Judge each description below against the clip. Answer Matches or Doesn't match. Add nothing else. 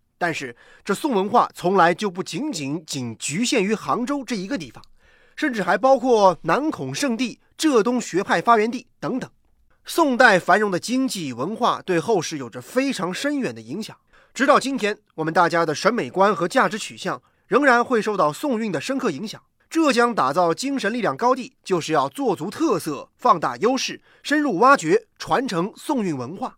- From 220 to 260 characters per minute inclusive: Doesn't match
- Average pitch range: Doesn't match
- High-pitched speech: Matches